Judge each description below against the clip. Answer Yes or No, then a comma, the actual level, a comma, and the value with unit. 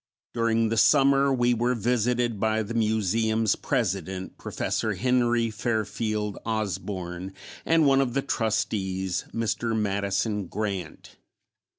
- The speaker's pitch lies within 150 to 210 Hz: No, low, 110 Hz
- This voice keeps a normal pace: No, slow, 110 wpm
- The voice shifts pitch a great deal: No, average, 3.1 semitones